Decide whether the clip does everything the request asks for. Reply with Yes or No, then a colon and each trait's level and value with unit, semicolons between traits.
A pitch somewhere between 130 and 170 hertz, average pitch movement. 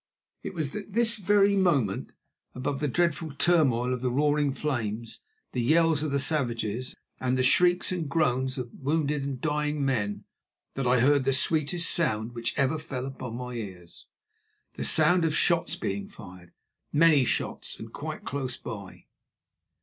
Yes: medium, 140 Hz; average, 4.5 semitones